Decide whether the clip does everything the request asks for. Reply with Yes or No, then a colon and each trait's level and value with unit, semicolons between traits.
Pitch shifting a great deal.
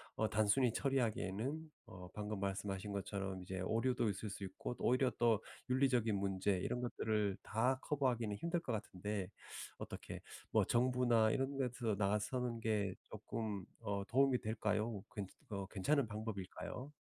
No: average, 3.8 semitones